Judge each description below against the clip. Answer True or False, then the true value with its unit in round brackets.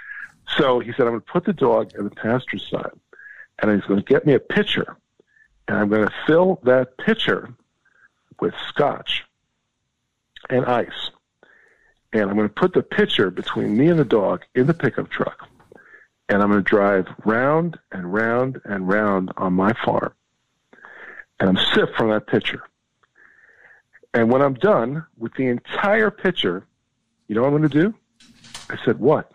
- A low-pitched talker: True (125 Hz)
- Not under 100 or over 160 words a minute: False (175 wpm)